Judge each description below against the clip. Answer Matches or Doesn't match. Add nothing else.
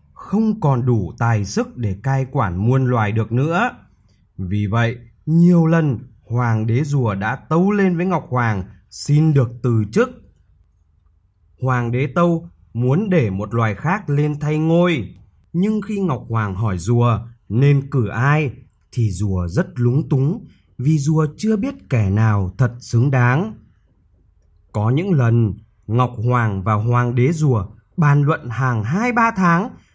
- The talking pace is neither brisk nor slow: Doesn't match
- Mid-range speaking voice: Doesn't match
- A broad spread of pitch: Matches